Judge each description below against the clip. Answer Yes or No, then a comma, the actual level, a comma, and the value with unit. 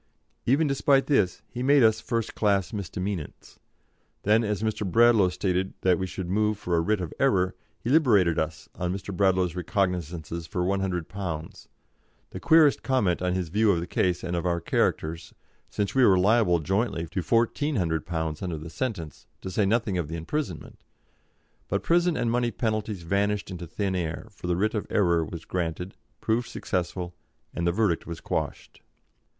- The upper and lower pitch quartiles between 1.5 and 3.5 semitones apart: No, average, 4.1 semitones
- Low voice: Yes, very low, 95 Hz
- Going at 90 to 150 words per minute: No, average, 170 wpm